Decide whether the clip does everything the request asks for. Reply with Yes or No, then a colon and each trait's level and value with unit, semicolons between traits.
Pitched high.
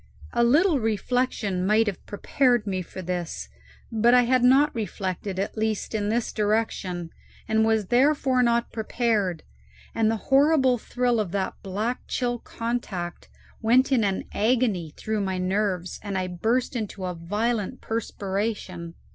Yes: high, 220 Hz